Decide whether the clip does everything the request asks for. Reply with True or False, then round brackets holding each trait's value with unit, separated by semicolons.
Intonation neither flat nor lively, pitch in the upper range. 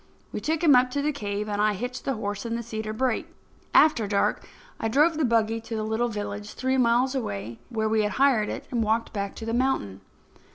True (3.4 semitones; 225 Hz)